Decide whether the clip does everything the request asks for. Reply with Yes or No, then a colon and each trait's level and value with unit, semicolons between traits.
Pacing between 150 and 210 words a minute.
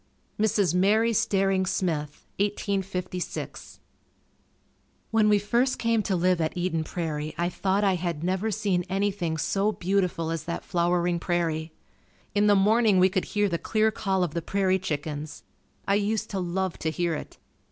Yes: average, 160 wpm